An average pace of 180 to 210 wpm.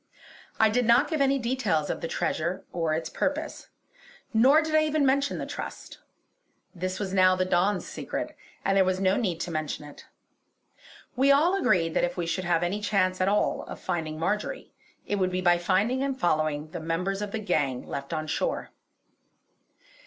Yes: average, 190 wpm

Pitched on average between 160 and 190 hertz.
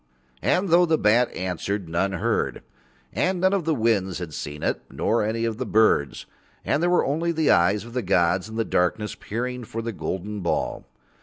No: low, 110 Hz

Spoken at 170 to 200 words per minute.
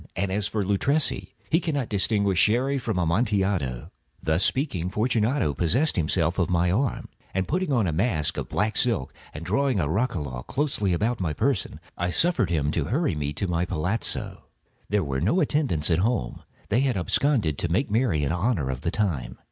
Yes: average, 180 wpm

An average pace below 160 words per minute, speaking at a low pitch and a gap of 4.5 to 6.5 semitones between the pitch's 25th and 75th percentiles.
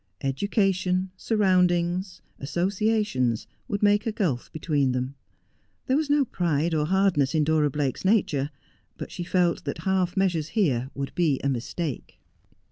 No: average, 140 wpm; medium, 175 Hz; average, 5.2 semitones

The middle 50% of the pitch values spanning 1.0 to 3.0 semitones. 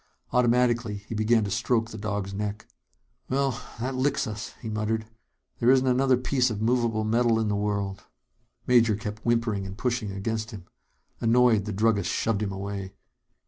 Yes: average, 2.7 semitones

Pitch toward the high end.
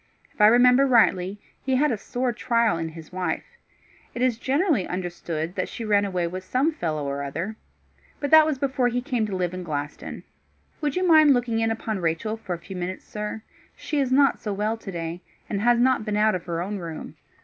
Yes: high, 215 Hz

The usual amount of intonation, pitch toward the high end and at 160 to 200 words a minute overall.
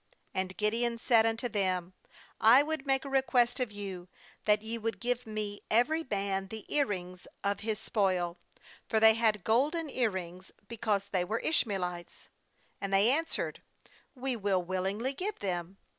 Yes: average, 4.2 semitones; high, 215 Hz; average, 175 wpm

